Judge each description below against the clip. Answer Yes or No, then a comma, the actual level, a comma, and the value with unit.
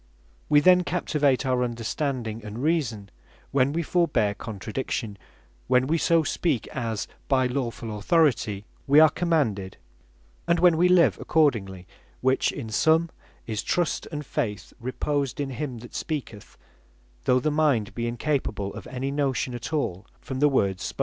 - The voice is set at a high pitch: No, low, 130 Hz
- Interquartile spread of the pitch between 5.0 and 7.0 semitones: Yes, average, 5.3 semitones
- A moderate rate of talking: Yes, average, 150 wpm